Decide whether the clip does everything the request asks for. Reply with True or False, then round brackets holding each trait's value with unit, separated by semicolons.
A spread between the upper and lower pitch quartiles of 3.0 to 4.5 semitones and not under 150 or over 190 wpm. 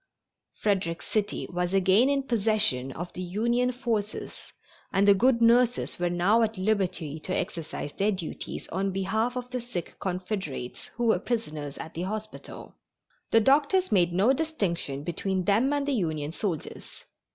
False (5.0 semitones; 155 wpm)